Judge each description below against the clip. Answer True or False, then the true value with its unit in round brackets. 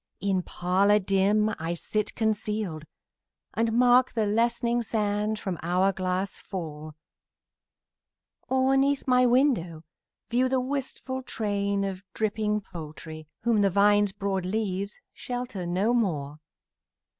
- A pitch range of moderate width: True (4.1 semitones)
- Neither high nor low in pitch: False (205 Hz)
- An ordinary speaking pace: False (120 wpm)